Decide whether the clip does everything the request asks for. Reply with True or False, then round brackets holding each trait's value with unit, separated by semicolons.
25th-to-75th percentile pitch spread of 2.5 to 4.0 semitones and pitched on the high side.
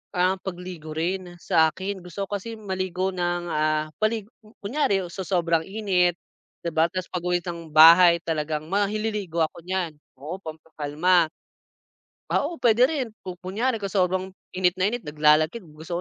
False (3.1 semitones; 180 Hz)